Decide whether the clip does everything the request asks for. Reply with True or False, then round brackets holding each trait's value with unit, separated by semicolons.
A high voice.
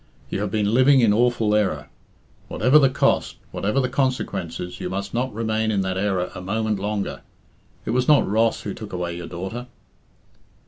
False (105 Hz)